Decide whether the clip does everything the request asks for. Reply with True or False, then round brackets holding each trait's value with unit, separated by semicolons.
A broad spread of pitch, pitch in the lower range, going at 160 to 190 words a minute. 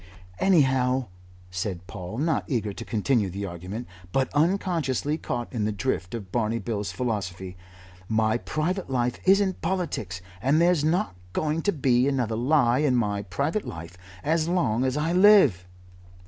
False (7.1 semitones; 125 Hz; 150 wpm)